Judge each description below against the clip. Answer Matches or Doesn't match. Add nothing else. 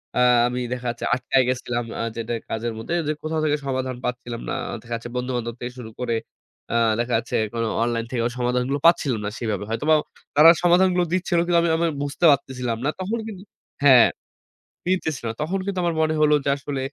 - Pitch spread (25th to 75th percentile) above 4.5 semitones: Matches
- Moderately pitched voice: Doesn't match